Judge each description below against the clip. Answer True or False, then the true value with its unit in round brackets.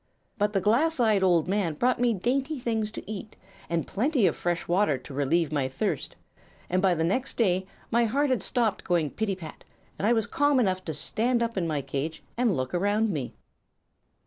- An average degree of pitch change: False (5.7 semitones)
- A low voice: False (200 Hz)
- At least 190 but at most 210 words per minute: True (200 wpm)